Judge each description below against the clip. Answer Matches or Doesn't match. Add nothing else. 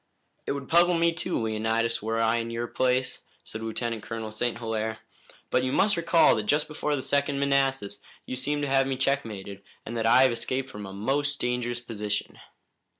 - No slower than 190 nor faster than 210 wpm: Matches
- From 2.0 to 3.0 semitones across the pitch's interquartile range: Doesn't match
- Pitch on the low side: Matches